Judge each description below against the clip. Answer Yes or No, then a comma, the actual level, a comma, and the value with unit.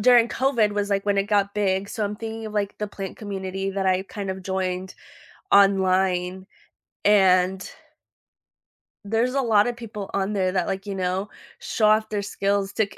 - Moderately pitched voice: No, high, 200 Hz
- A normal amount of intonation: No, narrow, 1.7 semitones